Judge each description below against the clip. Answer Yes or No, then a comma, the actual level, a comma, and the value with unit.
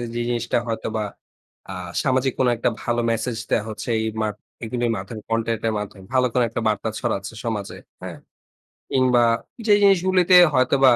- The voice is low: Yes, low, 120 Hz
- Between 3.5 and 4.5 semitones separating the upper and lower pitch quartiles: No, average, 2.7 semitones